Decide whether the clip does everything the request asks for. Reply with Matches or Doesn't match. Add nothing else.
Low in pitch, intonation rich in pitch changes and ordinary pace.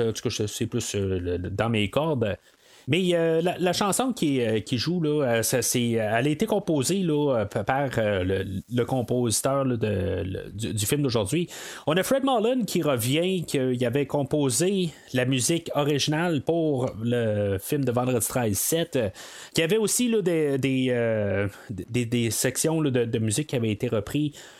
Doesn't match